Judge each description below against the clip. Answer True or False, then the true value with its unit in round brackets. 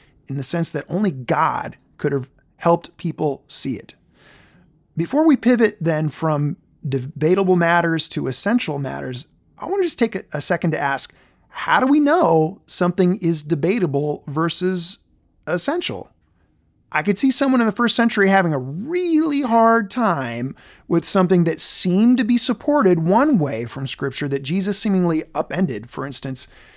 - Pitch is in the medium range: True (175 Hz)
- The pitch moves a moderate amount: False (7.2 semitones)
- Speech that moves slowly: False (155 wpm)